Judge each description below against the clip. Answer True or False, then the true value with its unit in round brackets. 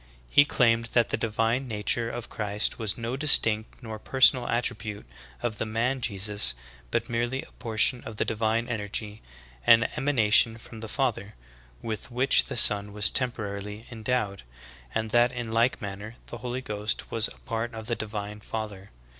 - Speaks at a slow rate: False (170 wpm)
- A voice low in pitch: True (115 Hz)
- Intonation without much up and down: True (2.3 semitones)